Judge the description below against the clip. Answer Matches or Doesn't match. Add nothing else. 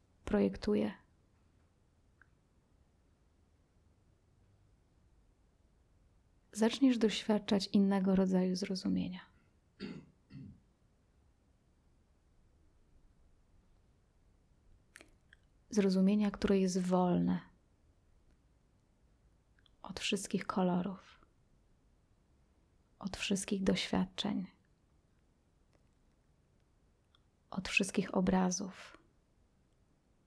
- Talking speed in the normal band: Doesn't match